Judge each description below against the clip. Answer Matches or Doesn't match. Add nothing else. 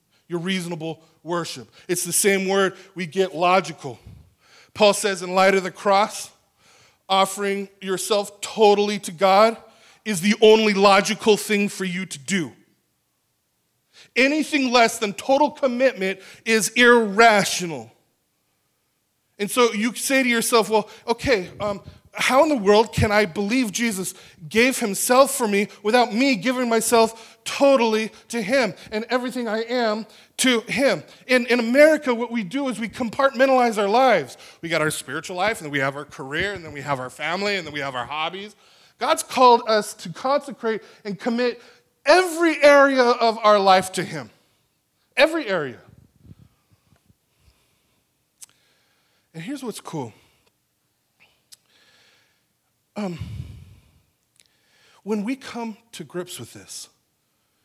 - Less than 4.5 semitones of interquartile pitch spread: Doesn't match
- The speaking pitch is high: Matches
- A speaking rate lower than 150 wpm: Matches